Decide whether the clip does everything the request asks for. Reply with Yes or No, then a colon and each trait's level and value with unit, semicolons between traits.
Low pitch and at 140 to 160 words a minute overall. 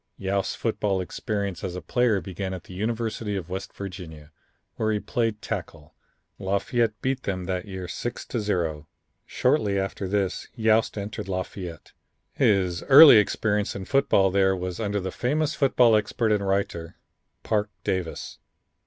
Yes: low, 100 Hz; average, 150 wpm